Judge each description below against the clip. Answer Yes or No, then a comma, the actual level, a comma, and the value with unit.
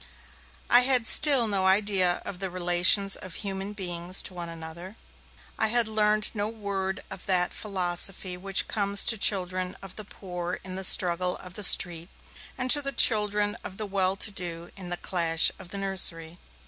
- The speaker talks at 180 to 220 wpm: Yes, average, 185 wpm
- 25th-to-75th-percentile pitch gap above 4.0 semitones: No, average, 2.7 semitones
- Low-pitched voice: No, high, 190 Hz